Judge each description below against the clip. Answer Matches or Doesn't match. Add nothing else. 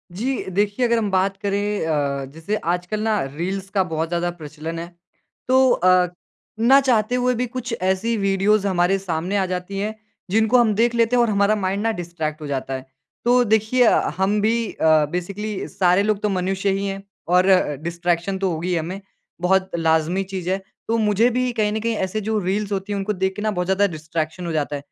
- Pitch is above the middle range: Matches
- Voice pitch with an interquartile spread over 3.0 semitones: Matches